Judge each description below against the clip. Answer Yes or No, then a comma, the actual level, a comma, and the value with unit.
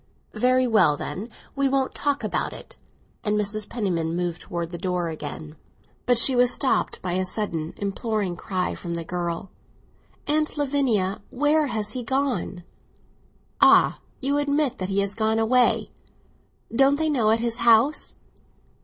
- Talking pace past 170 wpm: No, average, 155 wpm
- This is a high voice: Yes, high, 220 Hz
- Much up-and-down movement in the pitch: Yes, wide, 6.3 semitones